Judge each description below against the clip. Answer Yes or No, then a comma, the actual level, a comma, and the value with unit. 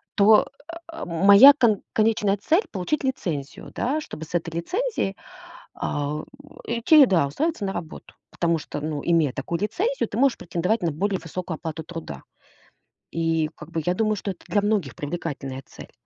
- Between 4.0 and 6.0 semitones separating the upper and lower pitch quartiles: Yes, wide, 5.4 semitones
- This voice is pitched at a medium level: Yes, medium, 180 Hz